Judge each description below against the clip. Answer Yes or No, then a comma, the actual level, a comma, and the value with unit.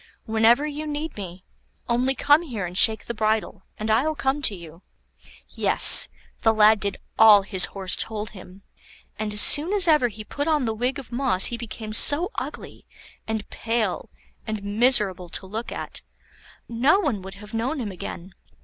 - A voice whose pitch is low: No, high, 220 Hz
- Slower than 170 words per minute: No, average, 175 wpm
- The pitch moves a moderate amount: Yes, average, 4.7 semitones